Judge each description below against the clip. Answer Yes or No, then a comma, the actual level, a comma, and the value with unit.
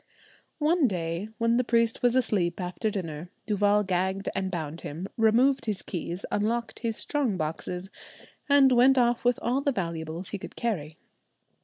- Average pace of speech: Yes, average, 160 wpm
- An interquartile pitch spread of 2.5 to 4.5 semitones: No, average, 5.2 semitones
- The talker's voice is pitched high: Yes, high, 210 Hz